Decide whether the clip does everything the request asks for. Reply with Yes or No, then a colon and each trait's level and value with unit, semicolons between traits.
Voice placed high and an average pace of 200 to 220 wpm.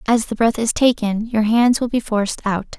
No: high, 225 Hz; fast, 235 wpm